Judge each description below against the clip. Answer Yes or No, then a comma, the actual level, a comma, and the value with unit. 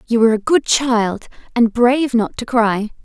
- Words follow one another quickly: No, average, 195 wpm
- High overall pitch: Yes, high, 235 Hz